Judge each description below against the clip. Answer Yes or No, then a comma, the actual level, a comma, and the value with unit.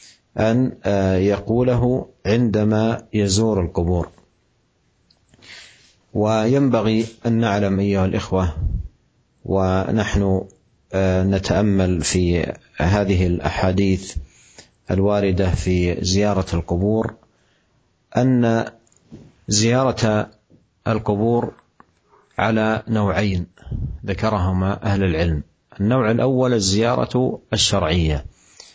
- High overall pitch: No, low, 100 Hz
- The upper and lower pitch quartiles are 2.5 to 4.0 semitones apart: Yes, average, 3.1 semitones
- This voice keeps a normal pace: No, slow, 65 wpm